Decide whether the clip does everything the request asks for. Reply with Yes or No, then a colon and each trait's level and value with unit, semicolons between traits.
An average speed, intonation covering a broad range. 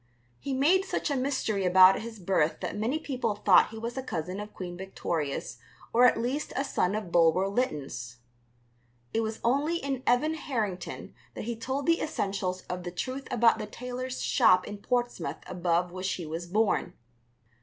Yes: average, 175 wpm; wide, 5.9 semitones